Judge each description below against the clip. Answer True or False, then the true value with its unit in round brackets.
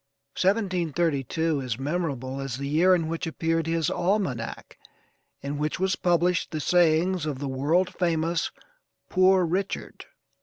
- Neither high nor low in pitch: True (165 Hz)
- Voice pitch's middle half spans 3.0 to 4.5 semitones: True (3.9 semitones)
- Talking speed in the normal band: False (130 wpm)